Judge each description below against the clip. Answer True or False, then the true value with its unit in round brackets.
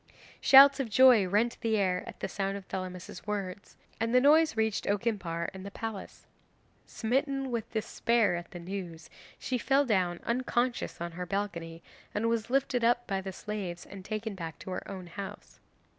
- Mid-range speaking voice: False (205 Hz)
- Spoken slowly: False (175 wpm)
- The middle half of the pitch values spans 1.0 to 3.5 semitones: False (4.3 semitones)